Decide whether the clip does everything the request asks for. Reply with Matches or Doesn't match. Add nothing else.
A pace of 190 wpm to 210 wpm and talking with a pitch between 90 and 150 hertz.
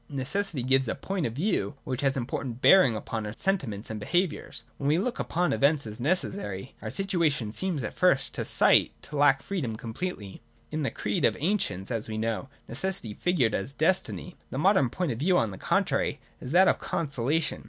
Matches